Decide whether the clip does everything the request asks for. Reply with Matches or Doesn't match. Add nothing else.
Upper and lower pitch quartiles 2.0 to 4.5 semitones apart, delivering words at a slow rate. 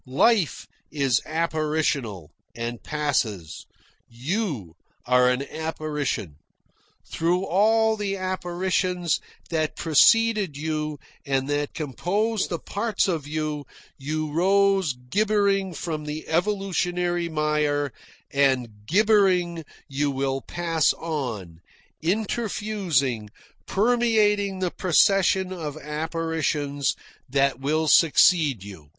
Doesn't match